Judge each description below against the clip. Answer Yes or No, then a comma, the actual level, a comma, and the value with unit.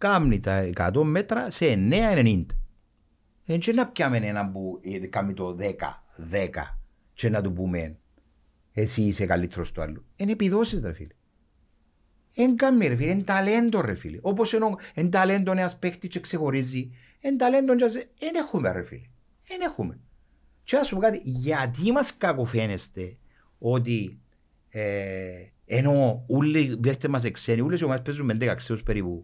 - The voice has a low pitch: Yes, low, 120 Hz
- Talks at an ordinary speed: Yes, average, 135 wpm